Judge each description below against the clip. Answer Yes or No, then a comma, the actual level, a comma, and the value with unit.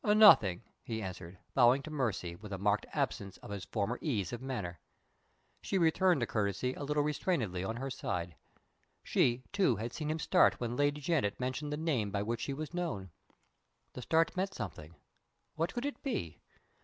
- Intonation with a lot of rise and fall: Yes, wide, 7.3 semitones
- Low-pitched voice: Yes, low, 125 Hz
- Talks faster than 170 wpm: Yes, average, 180 wpm